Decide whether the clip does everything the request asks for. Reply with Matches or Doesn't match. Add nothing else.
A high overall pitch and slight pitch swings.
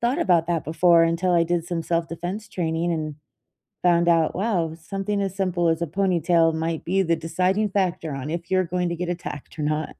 Doesn't match